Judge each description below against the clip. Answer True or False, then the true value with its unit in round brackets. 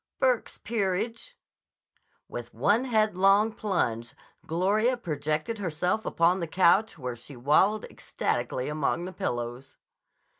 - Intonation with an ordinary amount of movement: False (6.3 semitones)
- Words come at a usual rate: False (110 wpm)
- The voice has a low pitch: False (185 Hz)